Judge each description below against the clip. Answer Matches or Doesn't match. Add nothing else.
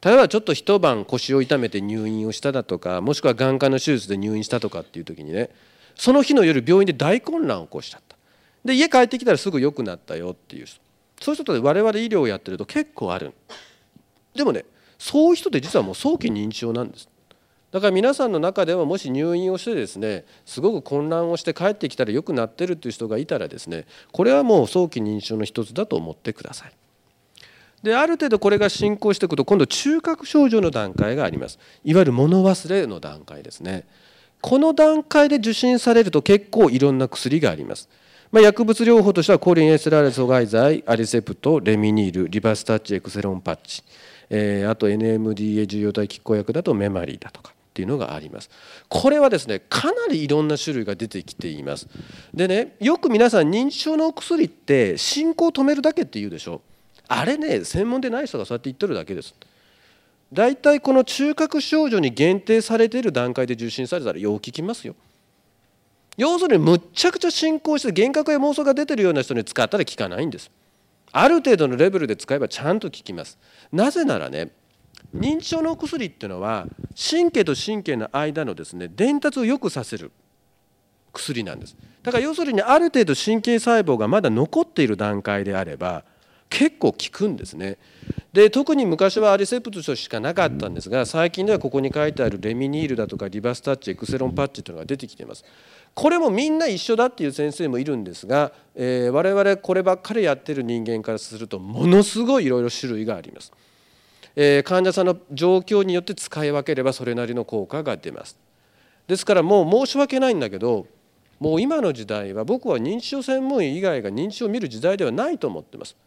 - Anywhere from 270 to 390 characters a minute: Doesn't match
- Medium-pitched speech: Matches